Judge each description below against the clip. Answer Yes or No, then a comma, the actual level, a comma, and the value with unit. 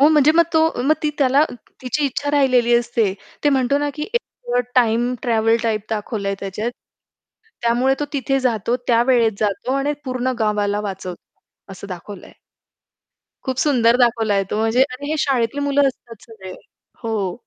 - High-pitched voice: Yes, high, 240 Hz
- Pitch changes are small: No, average, 3.8 semitones